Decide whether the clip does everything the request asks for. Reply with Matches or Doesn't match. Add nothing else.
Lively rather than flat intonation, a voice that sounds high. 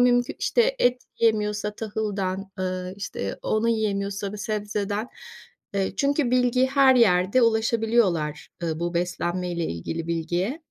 Doesn't match